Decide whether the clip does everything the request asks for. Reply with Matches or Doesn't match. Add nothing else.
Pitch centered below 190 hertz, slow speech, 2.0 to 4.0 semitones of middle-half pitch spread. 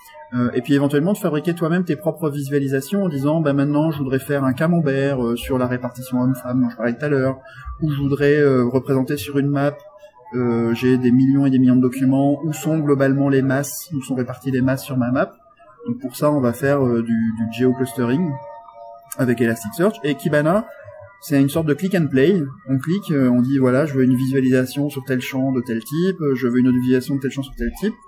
Doesn't match